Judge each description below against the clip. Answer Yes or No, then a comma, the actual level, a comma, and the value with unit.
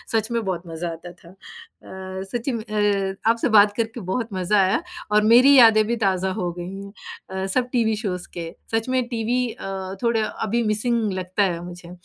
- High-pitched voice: Yes, high, 210 Hz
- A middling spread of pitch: Yes, average, 3.7 semitones